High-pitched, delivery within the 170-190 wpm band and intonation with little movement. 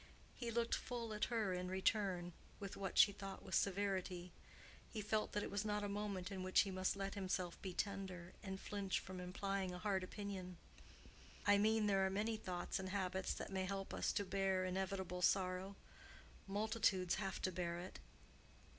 Yes: high, 195 Hz; average, 180 wpm; narrow, 1.7 semitones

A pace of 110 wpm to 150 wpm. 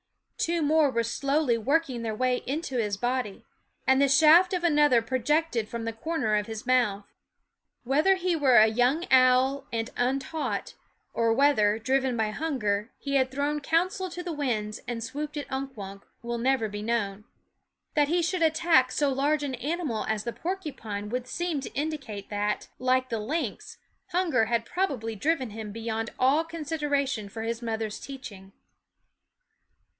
No: average, 165 wpm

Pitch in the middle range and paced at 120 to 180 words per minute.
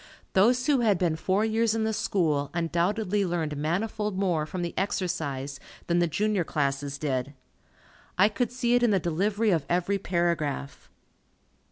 Yes: medium, 180 Hz; average, 160 wpm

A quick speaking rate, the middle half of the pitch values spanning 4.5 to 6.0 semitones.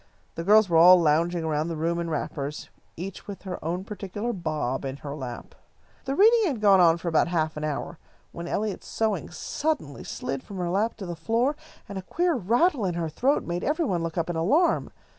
Yes: fast, 215 wpm; average, 4.9 semitones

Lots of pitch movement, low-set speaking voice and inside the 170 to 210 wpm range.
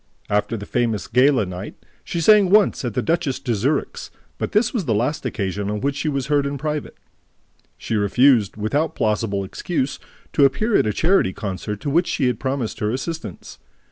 Yes: wide, 6.3 semitones; low, 130 Hz; average, 190 wpm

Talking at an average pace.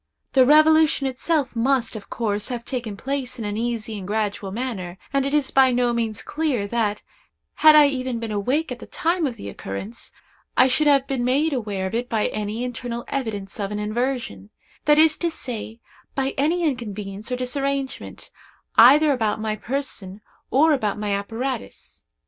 Yes: average, 175 wpm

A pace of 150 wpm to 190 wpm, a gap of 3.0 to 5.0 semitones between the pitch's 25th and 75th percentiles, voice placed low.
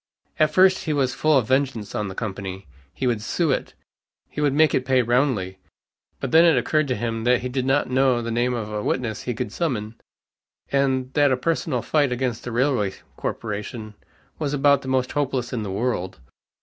No: average, 200 wpm; average, 3.8 semitones; low, 125 Hz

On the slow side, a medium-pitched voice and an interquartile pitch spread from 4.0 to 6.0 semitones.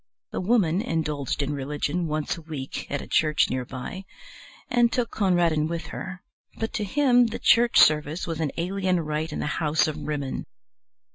No: average, 180 wpm; medium, 165 Hz; average, 4.4 semitones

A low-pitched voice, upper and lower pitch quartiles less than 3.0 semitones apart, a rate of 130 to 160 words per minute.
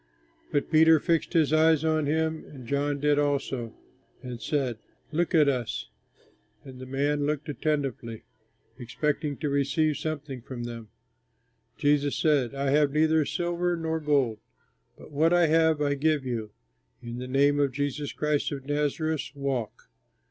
No: medium, 145 Hz; narrow, 2.6 semitones; average, 150 wpm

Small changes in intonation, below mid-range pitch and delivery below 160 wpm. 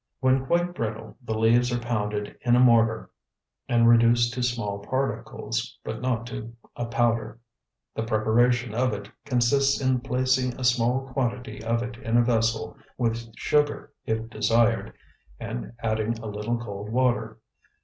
Yes: narrow, 1.9 semitones; low, 120 Hz; average, 150 wpm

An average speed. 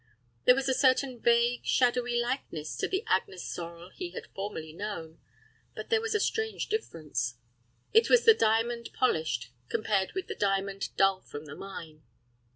Yes: average, 165 wpm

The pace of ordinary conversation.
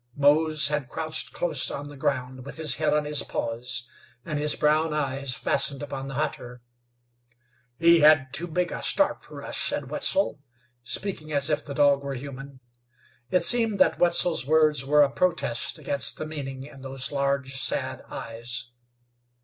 Yes: average, 165 wpm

